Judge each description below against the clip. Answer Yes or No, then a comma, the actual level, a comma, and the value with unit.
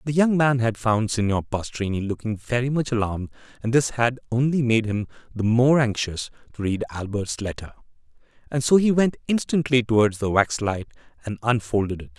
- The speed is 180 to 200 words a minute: No, average, 170 wpm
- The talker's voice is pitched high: No, low, 115 Hz